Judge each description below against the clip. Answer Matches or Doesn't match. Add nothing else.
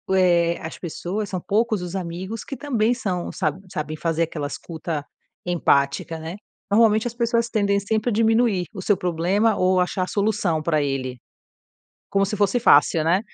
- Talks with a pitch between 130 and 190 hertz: Matches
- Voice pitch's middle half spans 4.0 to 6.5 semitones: Matches